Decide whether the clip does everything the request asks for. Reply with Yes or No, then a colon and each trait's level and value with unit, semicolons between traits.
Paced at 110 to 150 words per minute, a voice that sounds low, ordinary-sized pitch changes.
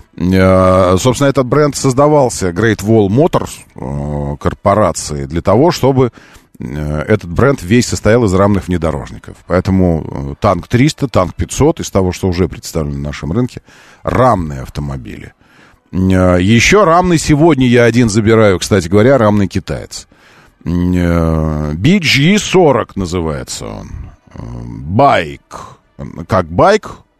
No: average, 125 wpm; very low, 95 Hz; wide, 6.5 semitones